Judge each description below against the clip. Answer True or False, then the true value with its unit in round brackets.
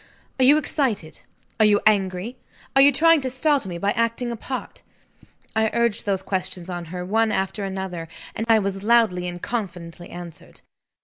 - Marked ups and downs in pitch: False (4.6 semitones)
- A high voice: True (205 Hz)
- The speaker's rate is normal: True (175 wpm)